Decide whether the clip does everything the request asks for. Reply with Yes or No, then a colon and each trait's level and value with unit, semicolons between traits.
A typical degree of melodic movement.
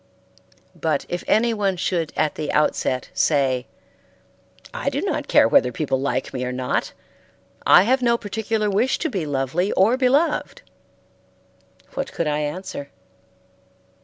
No: wide, 7.7 semitones